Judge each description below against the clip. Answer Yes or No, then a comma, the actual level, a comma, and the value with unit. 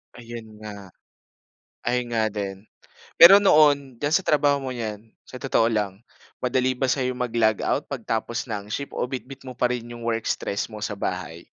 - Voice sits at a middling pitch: No, low, 120 Hz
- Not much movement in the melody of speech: No, average, 3.5 semitones